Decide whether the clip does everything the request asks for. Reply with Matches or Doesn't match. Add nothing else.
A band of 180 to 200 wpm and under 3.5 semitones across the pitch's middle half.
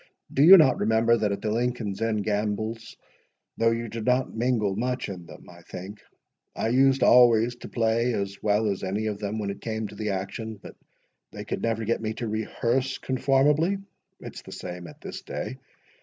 Matches